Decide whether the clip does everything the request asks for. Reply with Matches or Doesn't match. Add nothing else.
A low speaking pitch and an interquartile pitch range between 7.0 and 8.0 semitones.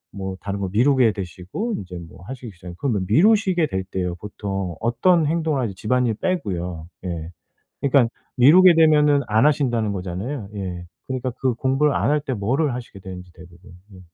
Matches